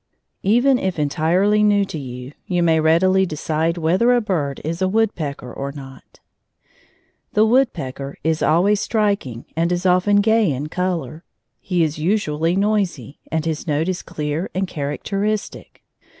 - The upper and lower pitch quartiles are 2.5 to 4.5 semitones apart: No, average, 4.9 semitones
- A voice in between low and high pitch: Yes, medium, 170 Hz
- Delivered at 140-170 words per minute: Yes, average, 150 wpm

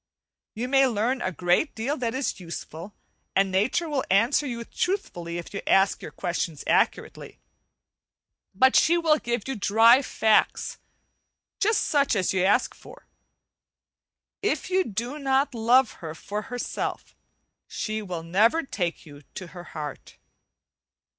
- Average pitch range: No, wide, 6.3 semitones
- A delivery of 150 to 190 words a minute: No, average, 140 wpm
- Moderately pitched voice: No, high, 225 Hz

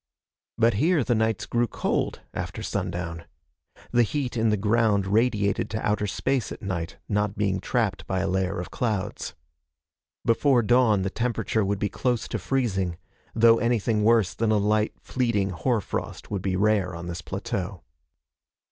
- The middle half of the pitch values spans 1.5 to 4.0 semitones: Yes, average, 3.3 semitones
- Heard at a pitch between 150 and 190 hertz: No, low, 105 Hz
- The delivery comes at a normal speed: Yes, average, 165 wpm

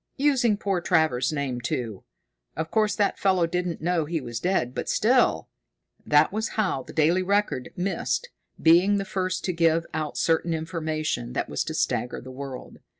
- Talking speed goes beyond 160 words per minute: Yes, average, 170 wpm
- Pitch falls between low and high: Yes, medium, 165 Hz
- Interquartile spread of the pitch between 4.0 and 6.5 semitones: Yes, average, 4.4 semitones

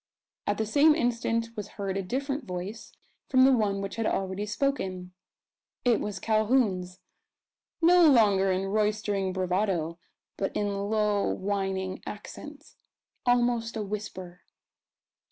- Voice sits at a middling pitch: No, high, 210 Hz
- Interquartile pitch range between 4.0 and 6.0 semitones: No, average, 3.3 semitones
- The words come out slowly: Yes, slow, 125 wpm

